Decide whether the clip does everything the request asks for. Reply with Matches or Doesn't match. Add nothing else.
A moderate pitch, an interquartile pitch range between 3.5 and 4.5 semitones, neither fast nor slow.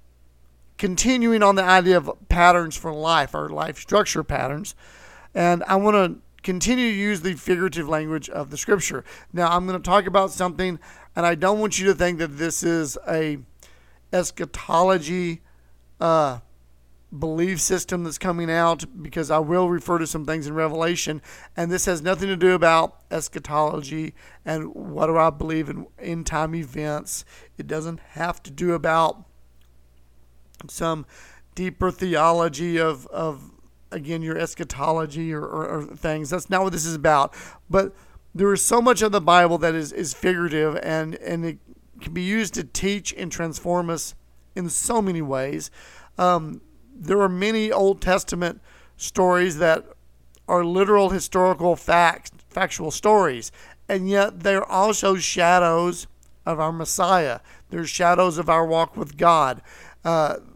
Doesn't match